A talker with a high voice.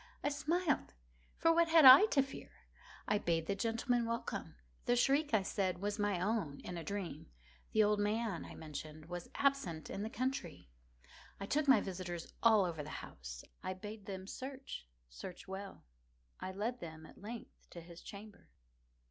Yes: high, 200 Hz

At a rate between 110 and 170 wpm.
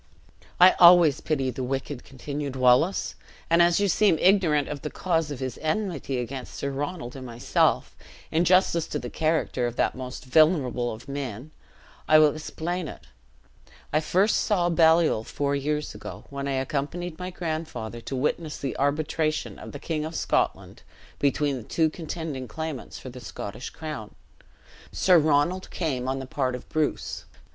Yes: average, 165 wpm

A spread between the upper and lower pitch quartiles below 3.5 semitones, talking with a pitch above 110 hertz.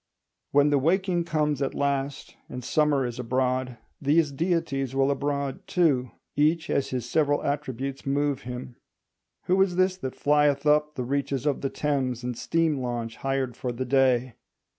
Yes: narrow, 2.6 semitones; medium, 140 Hz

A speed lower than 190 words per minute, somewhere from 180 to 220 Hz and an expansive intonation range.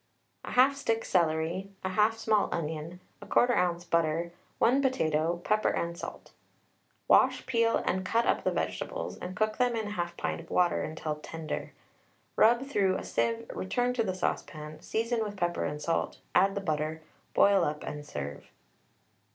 Yes: average, 160 wpm; medium, 185 Hz; wide, 5.7 semitones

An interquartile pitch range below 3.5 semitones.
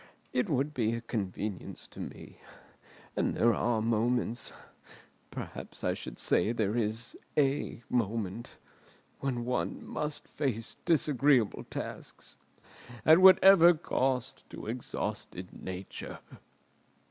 No: average, 4.0 semitones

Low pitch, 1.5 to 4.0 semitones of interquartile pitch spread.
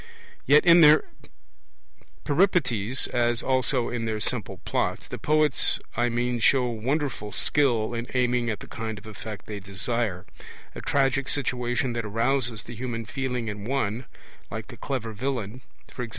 Yes: low, 120 Hz; average, 3.2 semitones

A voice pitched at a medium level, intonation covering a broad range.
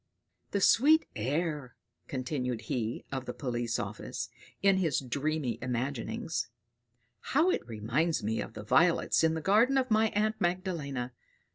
Yes: medium, 145 Hz; wide, 7.4 semitones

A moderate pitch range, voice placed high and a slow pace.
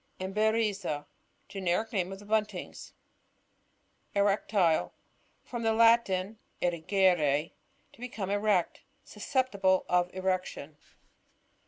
Yes: average, 3.3 semitones; high, 195 Hz; slow, 100 wpm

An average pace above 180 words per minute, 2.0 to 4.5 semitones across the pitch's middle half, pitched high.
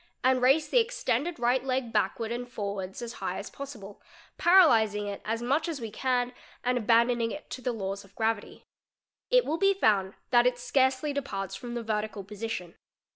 Yes: average, 190 wpm; average, 3.9 semitones; high, 240 Hz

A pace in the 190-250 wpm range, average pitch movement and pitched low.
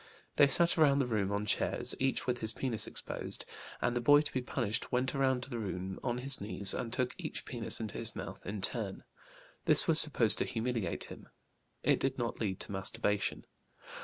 Yes: average, 195 wpm; average, 4.1 semitones; low, 120 Hz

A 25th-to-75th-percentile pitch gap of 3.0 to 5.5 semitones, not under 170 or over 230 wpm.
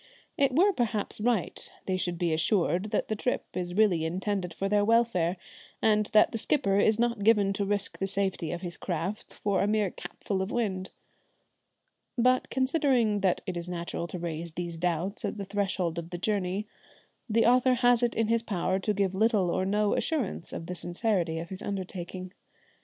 Yes: average, 3.6 semitones; average, 190 wpm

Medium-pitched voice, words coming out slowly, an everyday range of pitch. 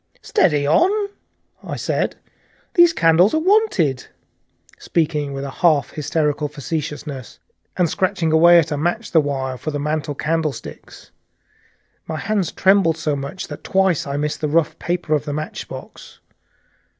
No: medium, 155 Hz; average, 145 wpm; average, 3.1 semitones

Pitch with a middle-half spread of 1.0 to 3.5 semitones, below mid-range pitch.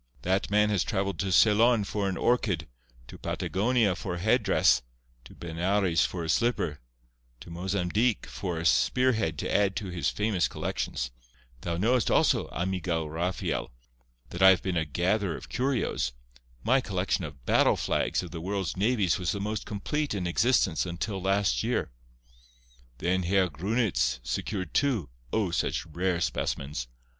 No: average, 4.3 semitones; very low, 95 Hz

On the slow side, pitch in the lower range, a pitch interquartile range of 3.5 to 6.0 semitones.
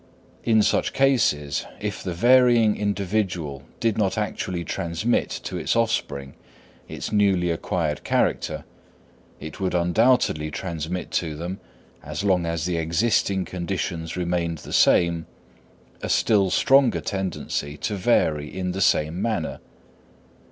Yes: slow, 125 wpm; very low, 90 Hz; average, 4.1 semitones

